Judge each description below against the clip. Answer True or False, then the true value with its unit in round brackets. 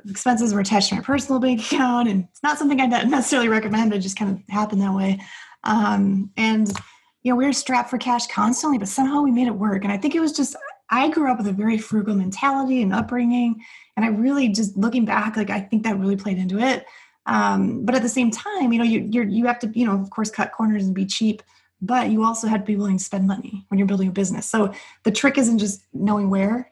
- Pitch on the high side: True (220 Hz)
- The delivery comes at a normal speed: False (250 wpm)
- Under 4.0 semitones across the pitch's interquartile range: True (3.6 semitones)